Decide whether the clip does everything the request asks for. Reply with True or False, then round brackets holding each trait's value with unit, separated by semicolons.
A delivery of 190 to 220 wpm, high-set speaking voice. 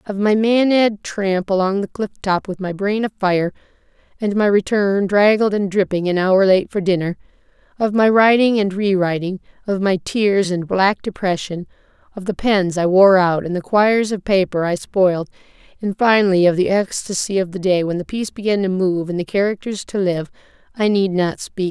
True (195 wpm; 195 Hz)